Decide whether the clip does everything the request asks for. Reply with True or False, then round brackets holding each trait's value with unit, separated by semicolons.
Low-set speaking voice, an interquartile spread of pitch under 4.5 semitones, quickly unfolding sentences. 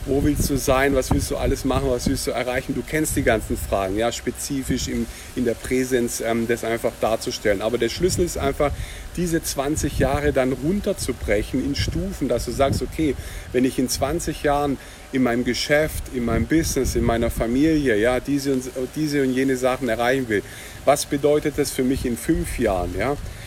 True (130 Hz; 3.4 semitones; 195 wpm)